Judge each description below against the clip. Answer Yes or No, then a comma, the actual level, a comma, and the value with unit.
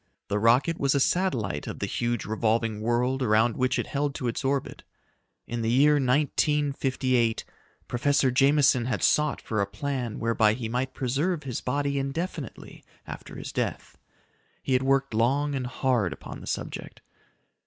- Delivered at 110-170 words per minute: Yes, average, 160 wpm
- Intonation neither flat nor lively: Yes, average, 3.3 semitones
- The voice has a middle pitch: No, low, 130 Hz